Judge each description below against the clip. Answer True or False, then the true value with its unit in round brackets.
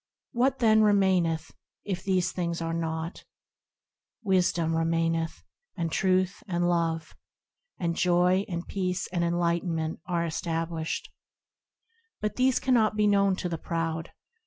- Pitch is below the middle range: False (175 Hz)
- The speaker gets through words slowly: True (130 wpm)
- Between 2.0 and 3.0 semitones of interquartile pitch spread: True (2.6 semitones)